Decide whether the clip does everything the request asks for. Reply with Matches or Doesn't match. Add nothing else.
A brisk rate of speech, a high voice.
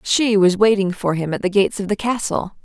Matches